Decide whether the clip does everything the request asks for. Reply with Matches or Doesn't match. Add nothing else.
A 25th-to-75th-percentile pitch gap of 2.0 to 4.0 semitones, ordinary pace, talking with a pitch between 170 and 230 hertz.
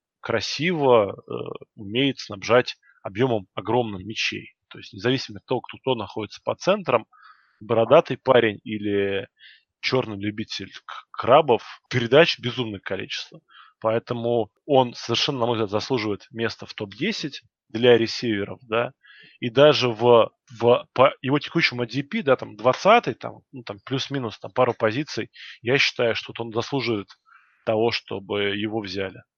Doesn't match